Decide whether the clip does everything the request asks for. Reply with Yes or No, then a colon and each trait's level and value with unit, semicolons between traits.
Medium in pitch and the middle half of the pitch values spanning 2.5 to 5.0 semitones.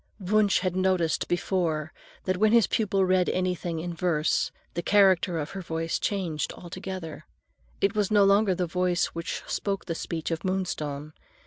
Yes: medium, 180 Hz; average, 2.8 semitones